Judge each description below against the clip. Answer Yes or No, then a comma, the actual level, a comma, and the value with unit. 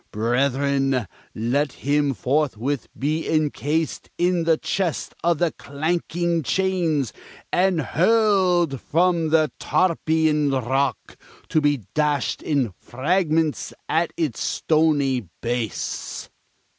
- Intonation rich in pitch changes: No, average, 3.5 semitones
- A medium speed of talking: No, slow, 100 wpm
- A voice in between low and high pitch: Yes, medium, 150 Hz